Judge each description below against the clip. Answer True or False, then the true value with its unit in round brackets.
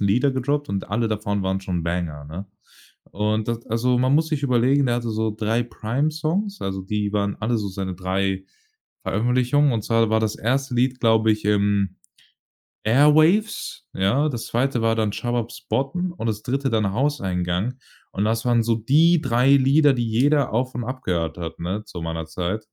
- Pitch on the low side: True (115 Hz)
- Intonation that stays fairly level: False (4.6 semitones)